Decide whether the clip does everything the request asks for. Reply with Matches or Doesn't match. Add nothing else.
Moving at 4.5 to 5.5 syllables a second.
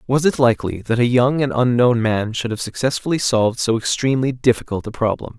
Doesn't match